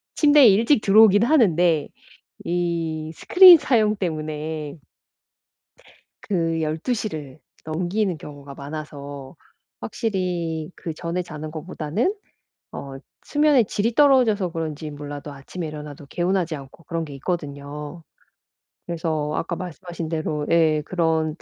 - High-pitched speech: No, medium, 165 Hz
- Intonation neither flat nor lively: Yes, average, 4.0 semitones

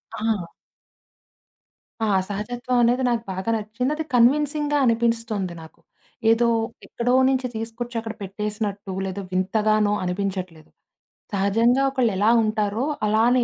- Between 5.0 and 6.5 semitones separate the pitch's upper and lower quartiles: No, average, 3.1 semitones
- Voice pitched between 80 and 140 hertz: No, high, 225 Hz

